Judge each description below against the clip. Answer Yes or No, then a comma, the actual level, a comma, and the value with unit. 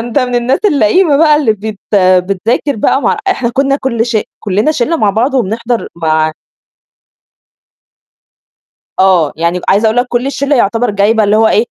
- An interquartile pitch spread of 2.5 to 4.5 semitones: No, average, 4.9 semitones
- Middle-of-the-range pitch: No, high, 230 Hz